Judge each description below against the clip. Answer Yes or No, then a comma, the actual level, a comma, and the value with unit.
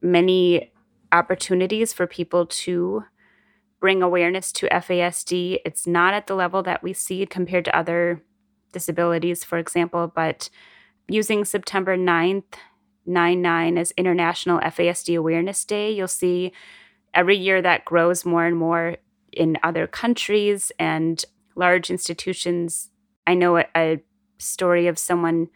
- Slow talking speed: Yes, slow, 130 wpm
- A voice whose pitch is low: No, medium, 180 Hz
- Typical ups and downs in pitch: No, narrow, 2.0 semitones